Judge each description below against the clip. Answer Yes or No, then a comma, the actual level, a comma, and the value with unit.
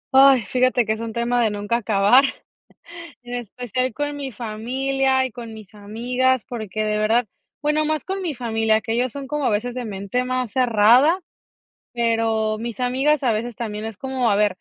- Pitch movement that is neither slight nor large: Yes, average, 3.0 semitones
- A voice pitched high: Yes, high, 240 Hz